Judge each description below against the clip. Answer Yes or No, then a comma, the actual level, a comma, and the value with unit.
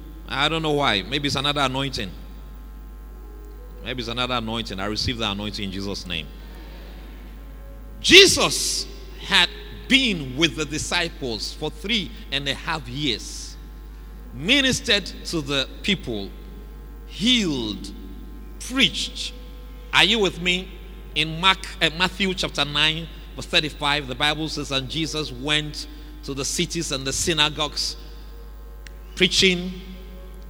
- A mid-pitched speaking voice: Yes, medium, 150 Hz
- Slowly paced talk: Yes, slow, 120 wpm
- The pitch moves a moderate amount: No, wide, 5.8 semitones